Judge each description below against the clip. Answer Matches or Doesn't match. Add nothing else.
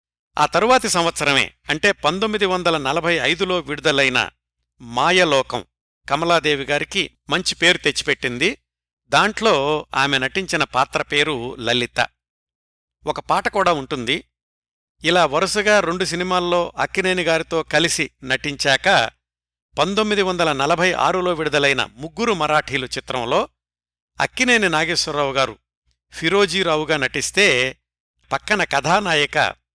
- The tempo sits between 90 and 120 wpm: Matches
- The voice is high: Doesn't match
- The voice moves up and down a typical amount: Doesn't match